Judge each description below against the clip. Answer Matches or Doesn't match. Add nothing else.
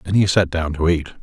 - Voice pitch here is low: Matches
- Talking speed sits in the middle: Doesn't match